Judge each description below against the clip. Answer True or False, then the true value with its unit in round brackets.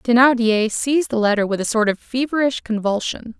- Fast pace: False (175 wpm)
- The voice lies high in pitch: True (235 Hz)